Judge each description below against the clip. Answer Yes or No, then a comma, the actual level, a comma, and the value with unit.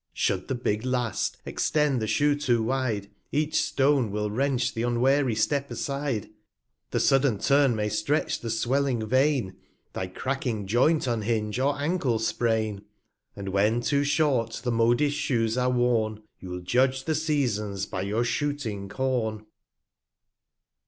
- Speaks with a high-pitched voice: No, low, 120 Hz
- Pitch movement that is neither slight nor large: Yes, average, 4.2 semitones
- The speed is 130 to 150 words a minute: Yes, average, 145 wpm